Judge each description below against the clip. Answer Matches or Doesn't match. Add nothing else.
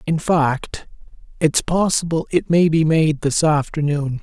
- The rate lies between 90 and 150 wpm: Matches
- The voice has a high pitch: Doesn't match